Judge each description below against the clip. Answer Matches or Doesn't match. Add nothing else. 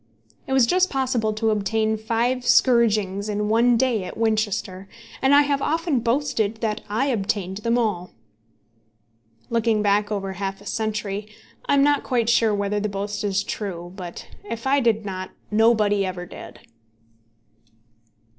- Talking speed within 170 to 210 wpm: Doesn't match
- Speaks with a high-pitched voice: Matches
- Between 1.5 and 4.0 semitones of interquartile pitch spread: Matches